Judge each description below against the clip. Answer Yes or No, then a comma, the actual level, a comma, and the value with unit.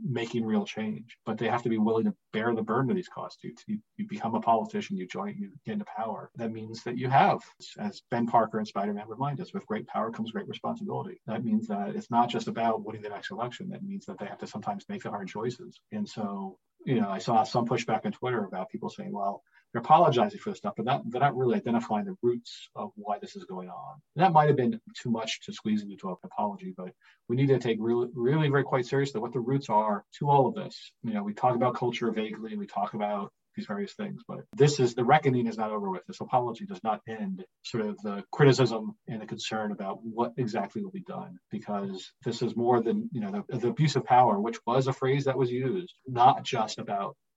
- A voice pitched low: Yes, low, 125 Hz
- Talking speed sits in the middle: No, fast, 245 wpm